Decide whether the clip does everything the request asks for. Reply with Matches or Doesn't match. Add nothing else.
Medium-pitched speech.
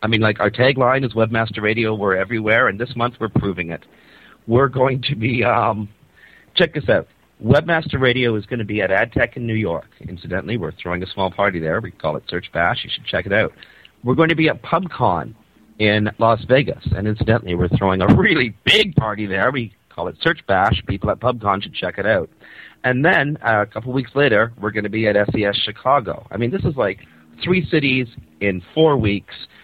Doesn't match